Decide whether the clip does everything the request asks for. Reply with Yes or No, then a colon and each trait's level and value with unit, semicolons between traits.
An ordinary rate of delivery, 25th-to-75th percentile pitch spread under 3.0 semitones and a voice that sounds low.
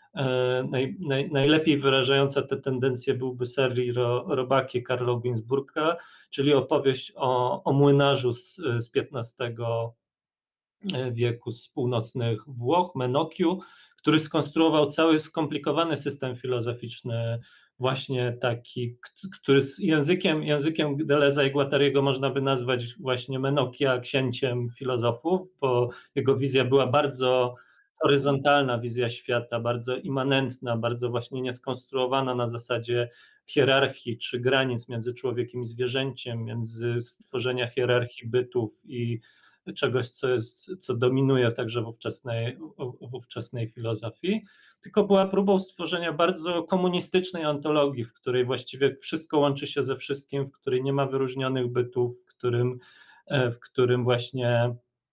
Yes: average, 120 wpm; narrow, 2.6 semitones; low, 130 Hz